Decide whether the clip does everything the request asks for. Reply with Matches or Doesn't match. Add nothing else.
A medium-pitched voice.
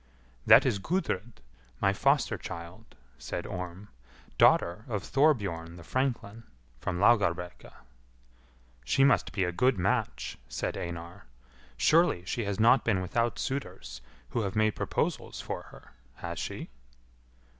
Doesn't match